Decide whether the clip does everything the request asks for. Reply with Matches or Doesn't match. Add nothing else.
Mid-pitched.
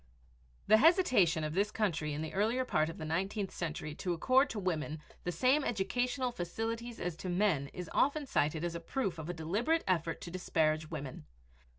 Matches